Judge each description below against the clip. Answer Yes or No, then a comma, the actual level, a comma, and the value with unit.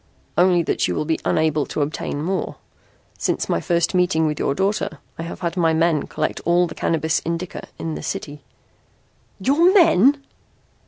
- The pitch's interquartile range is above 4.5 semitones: No, average, 2.7 semitones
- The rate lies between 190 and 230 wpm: No, average, 170 wpm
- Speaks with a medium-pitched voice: Yes, medium, 165 Hz